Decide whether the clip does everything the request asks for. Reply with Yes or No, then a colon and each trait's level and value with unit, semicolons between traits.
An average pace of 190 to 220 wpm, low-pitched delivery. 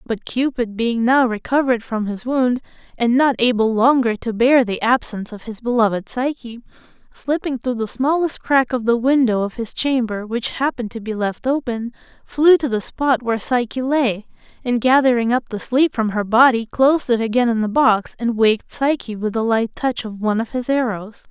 No: average, 195 wpm; high, 240 Hz